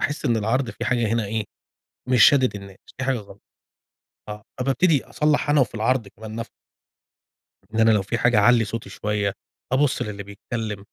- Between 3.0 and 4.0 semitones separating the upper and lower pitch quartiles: Yes, average, 3.5 semitones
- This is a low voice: Yes, low, 115 Hz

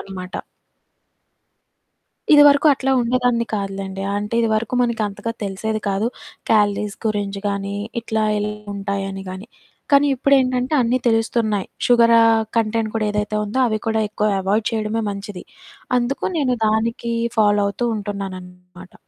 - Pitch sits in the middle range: No, high, 215 Hz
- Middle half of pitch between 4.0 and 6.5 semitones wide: No, average, 2.7 semitones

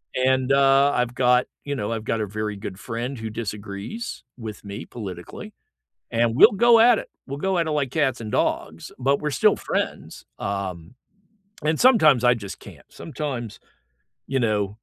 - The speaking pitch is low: Yes, low, 125 Hz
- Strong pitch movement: No, average, 4.9 semitones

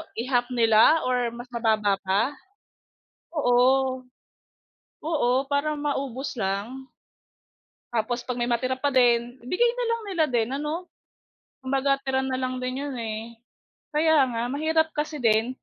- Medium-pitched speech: No, very high, 255 Hz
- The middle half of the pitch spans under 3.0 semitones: No, average, 3.3 semitones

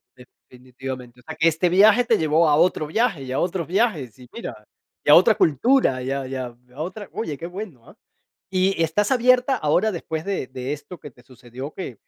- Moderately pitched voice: Yes, medium, 155 Hz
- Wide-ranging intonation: Yes, wide, 7.1 semitones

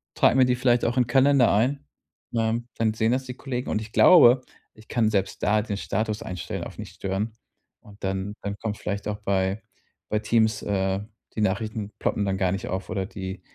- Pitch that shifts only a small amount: No, average, 3.2 semitones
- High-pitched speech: No, low, 110 Hz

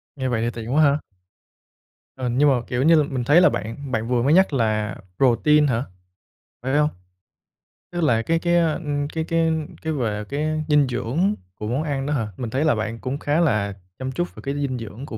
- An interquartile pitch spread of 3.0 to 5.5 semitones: Yes, average, 4.5 semitones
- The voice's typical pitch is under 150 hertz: Yes, low, 135 Hz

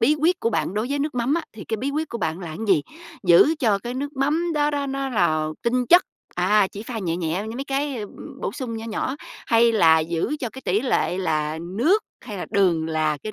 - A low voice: No, high, 225 Hz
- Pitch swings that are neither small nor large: No, wide, 7.3 semitones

